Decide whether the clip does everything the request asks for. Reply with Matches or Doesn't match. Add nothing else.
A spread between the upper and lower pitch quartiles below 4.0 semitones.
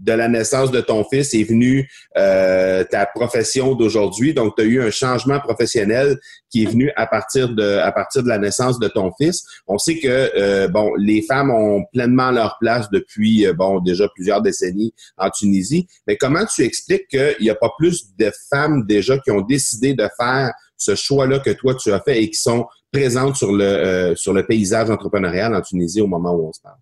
Doesn't match